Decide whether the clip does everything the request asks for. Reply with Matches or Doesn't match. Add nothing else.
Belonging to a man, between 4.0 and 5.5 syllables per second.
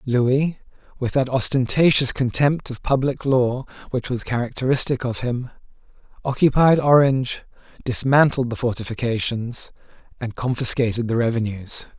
Matches